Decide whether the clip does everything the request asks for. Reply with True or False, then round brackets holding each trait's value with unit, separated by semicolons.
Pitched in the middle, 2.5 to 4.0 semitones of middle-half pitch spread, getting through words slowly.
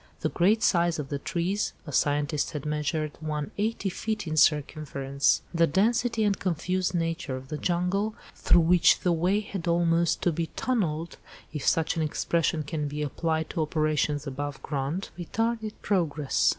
False (165 Hz; 3.4 semitones; 165 wpm)